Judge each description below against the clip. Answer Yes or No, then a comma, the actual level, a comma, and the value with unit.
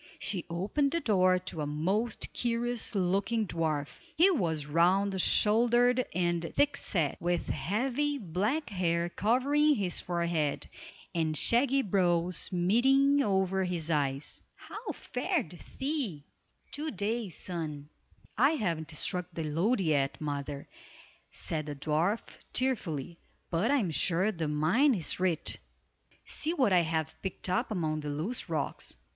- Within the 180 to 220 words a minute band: No, slow, 135 wpm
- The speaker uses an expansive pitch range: Yes, wide, 6.6 semitones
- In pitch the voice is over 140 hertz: Yes, medium, 185 Hz